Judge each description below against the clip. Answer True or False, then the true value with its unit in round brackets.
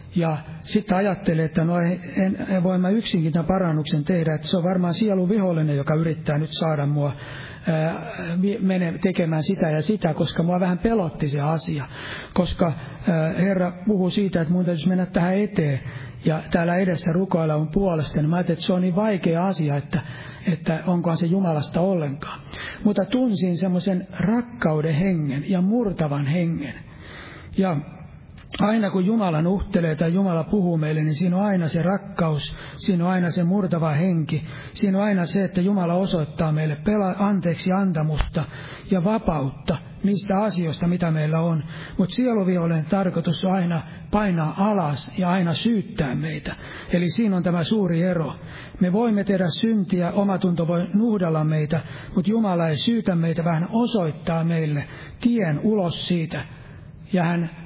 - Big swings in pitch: False (3.4 semitones)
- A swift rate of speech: True (160 wpm)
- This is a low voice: False (175 Hz)